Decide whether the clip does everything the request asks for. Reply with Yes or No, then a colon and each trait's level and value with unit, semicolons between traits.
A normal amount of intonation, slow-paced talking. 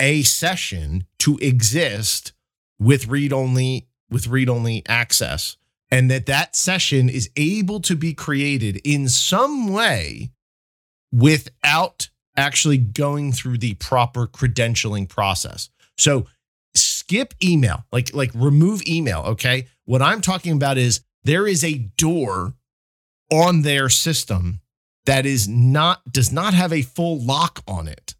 Yes: average, 4.9 semitones; slow, 130 wpm